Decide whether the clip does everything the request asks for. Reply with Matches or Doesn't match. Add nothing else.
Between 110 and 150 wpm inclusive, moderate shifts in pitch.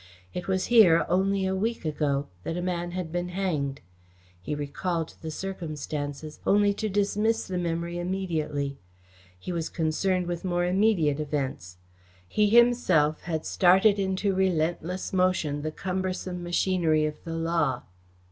Matches